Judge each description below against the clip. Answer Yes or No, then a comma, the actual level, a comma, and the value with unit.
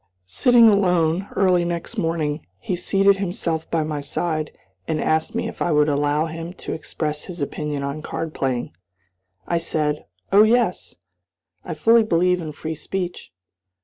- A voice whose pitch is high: No, medium, 165 Hz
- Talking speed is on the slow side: No, average, 155 wpm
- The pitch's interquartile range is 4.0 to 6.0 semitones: No, average, 3.0 semitones